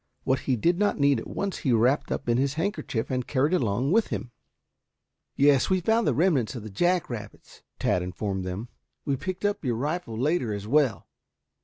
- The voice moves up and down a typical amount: No, wide, 7.3 semitones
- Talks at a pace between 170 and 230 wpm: Yes, average, 200 wpm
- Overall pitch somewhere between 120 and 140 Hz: Yes, low, 135 Hz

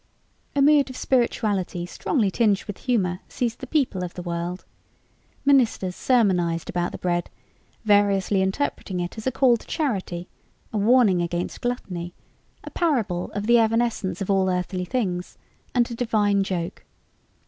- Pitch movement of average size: Yes, average, 5.0 semitones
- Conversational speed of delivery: Yes, average, 150 wpm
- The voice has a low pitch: No, high, 200 Hz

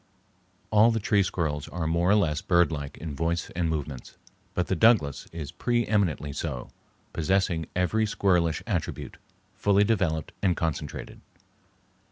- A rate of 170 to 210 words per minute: No, average, 140 wpm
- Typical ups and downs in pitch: Yes, average, 4.3 semitones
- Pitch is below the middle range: Yes, very low, 85 Hz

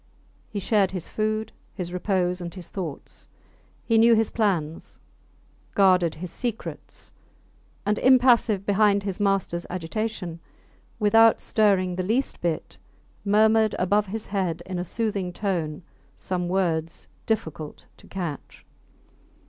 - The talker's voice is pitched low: No, high, 195 Hz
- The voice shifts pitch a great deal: No, average, 3.4 semitones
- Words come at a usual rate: No, slow, 125 wpm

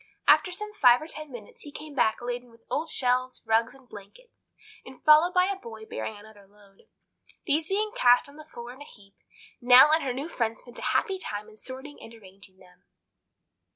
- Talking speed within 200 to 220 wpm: Yes, fast, 205 wpm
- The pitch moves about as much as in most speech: No, wide, 5.8 semitones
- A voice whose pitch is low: No, very high, 250 Hz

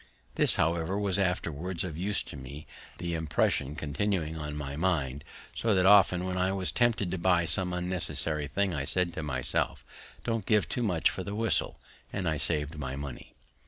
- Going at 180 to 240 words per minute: Yes, average, 185 wpm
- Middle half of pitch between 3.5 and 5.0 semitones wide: Yes, average, 4.1 semitones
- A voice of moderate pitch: No, very low, 85 Hz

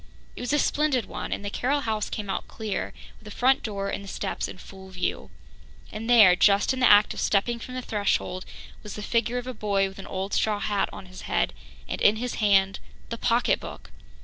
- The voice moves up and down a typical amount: Yes, average, 3.5 semitones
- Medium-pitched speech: No, high, 210 Hz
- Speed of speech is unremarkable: No, fast, 225 wpm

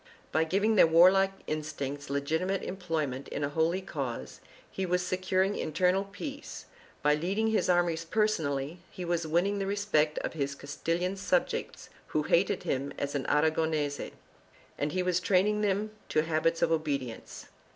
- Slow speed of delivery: No, average, 150 wpm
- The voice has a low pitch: No, medium, 165 Hz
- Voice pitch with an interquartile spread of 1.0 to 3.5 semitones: No, average, 4.2 semitones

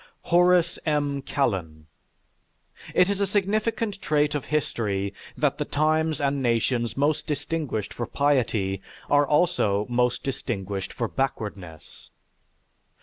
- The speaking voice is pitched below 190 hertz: Yes, medium, 140 Hz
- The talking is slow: Yes, slow, 115 wpm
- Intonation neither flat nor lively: No, wide, 6.4 semitones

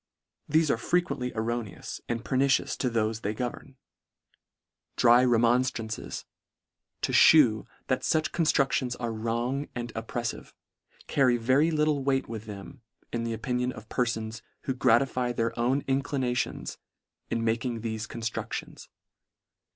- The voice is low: Yes, low, 120 Hz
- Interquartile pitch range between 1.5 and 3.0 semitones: Yes, average, 2.7 semitones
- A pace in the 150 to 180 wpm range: No, slow, 135 wpm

